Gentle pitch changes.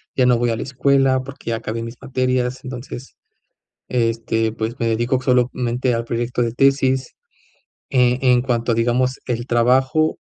Yes: narrow, 1.8 semitones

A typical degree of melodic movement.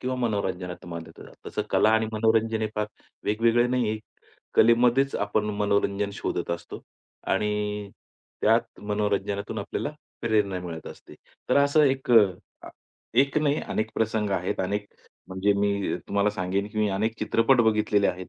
No: narrow, 2.1 semitones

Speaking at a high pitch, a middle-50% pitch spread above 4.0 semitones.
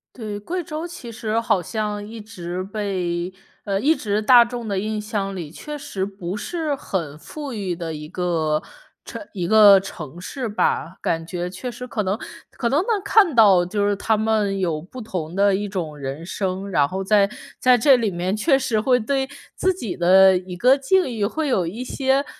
Yes: high, 205 Hz; average, 5.1 semitones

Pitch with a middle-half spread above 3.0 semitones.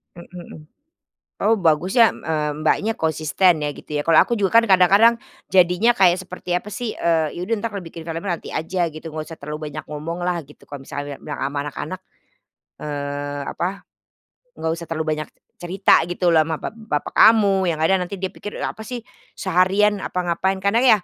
Yes: average, 3.8 semitones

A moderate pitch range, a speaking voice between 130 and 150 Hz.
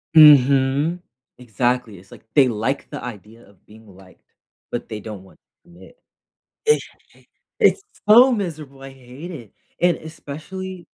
No: wide, 7.0 semitones; low, 135 Hz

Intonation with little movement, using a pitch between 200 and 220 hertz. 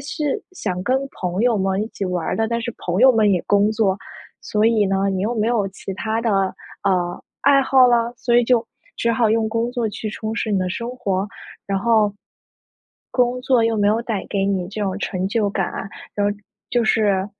No: average, 3.2 semitones; high, 215 Hz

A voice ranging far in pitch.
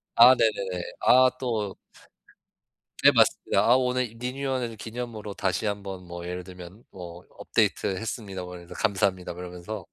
No: average, 4.6 semitones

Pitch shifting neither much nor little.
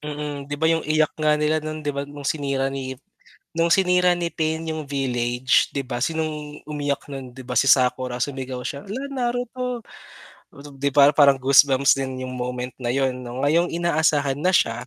Yes: average, 3.2 semitones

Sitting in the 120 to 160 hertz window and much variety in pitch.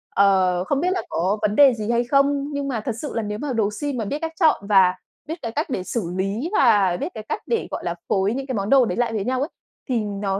No: high, 230 Hz; wide, 5.7 semitones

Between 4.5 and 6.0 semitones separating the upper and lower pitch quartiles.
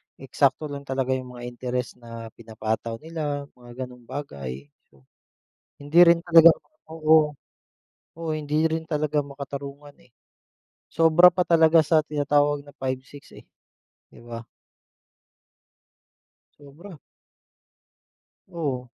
No: average, 3.9 semitones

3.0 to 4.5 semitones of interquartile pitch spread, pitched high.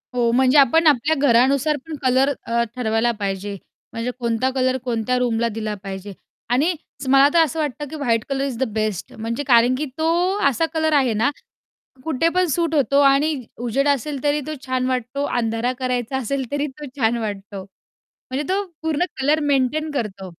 Yes: average, 3.9 semitones; very high, 260 Hz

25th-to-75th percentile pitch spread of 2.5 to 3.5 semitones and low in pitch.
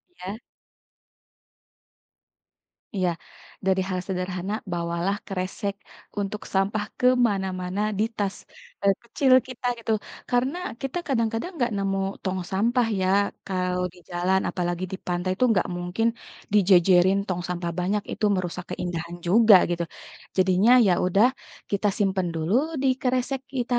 No: average, 3.2 semitones; high, 190 Hz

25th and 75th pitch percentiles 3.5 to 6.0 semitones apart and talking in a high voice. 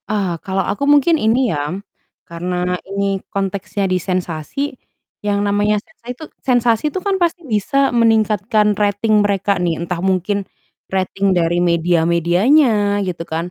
Yes: average, 3.8 semitones; high, 200 Hz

